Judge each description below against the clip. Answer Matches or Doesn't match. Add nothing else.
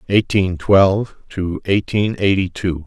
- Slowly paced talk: Matches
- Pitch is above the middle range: Doesn't match